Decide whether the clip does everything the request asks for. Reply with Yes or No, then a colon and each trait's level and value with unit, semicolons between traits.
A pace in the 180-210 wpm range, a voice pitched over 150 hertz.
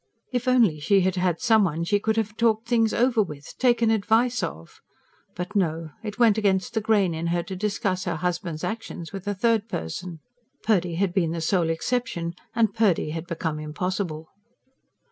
Yes: average, 185 wpm; high, 190 Hz